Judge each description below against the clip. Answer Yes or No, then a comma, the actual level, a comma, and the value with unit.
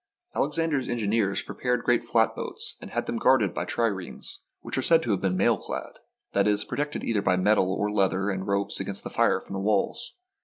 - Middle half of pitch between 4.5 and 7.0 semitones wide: No, average, 3.7 semitones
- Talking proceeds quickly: Yes, fast, 215 wpm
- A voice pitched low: Yes, low, 105 Hz